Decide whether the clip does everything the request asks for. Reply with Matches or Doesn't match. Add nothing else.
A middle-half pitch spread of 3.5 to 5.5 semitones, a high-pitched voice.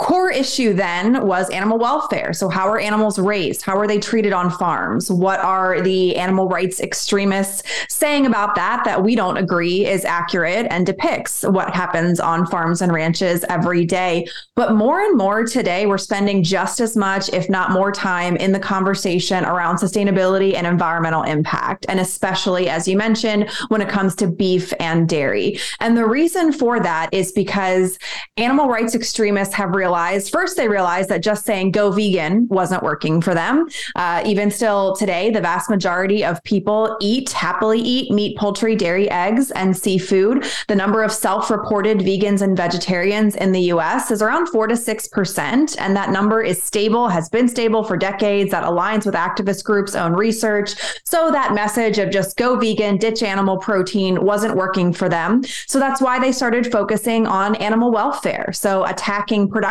Doesn't match